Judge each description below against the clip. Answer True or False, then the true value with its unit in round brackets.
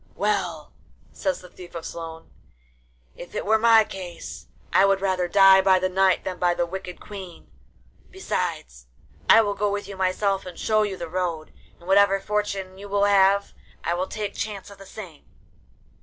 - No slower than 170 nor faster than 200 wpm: True (180 wpm)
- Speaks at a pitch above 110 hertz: True (190 Hz)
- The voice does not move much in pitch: True (2.1 semitones)